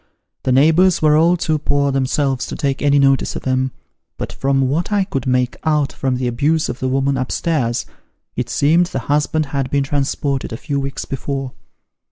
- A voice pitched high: No, medium, 140 Hz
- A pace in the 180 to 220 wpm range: Yes, average, 195 wpm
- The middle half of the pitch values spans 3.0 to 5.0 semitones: No, narrow, 2.4 semitones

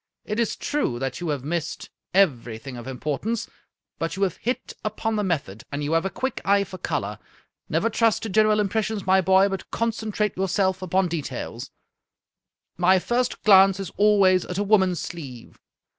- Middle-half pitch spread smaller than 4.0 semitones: No, average, 4.3 semitones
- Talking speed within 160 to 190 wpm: Yes, average, 175 wpm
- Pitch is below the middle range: No, high, 190 Hz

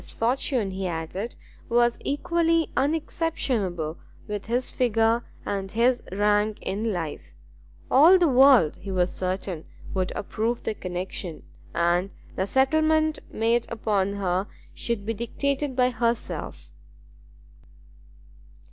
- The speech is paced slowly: Yes, slow, 115 wpm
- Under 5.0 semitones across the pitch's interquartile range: No, average, 5.3 semitones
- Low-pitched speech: No, high, 225 Hz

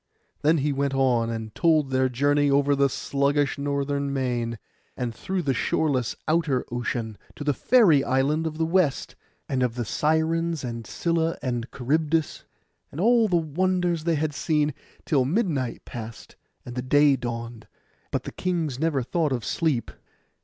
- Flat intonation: No, average, 4.2 semitones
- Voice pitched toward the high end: No, medium, 140 Hz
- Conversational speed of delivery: Yes, average, 160 wpm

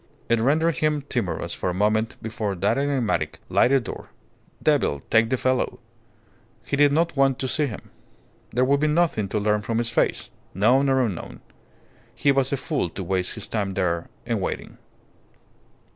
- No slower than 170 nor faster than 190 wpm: Yes, average, 175 wpm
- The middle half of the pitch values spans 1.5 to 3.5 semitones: No, average, 5.1 semitones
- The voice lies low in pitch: Yes, low, 120 Hz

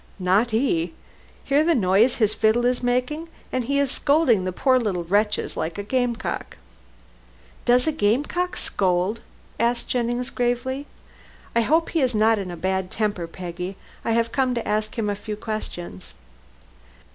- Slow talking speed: No, average, 170 wpm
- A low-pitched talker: No, high, 225 Hz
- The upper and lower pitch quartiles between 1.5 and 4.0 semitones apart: No, average, 4.4 semitones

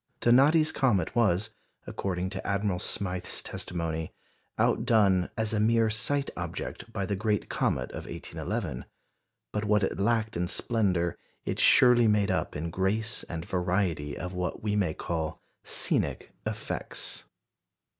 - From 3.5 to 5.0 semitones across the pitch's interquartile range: Yes, average, 3.8 semitones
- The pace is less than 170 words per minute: Yes, slow, 135 wpm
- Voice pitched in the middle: No, low, 100 Hz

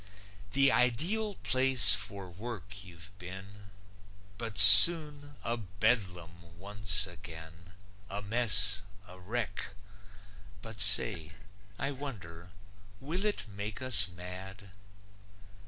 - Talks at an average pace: No, slow, 100 wpm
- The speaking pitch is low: Yes, low, 100 Hz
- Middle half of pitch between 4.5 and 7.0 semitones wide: Yes, average, 4.8 semitones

